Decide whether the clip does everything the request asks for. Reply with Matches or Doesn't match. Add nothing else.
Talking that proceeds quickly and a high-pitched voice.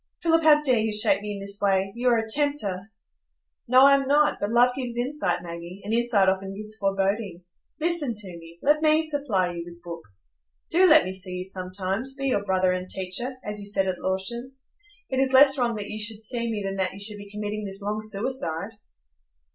Matches